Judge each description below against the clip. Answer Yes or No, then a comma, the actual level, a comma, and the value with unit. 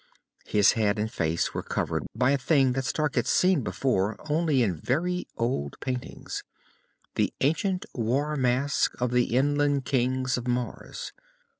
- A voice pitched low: Yes, low, 130 Hz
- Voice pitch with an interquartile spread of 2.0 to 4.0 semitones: Yes, average, 3.3 semitones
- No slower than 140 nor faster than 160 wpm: Yes, average, 150 wpm